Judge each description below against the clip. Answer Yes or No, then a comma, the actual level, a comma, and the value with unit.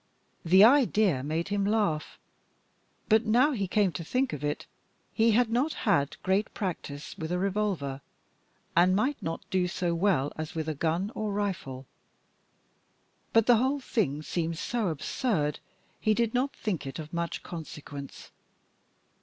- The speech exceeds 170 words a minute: No, average, 155 wpm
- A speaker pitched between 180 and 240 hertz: Yes, medium, 185 Hz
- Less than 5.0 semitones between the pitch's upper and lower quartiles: No, wide, 5.6 semitones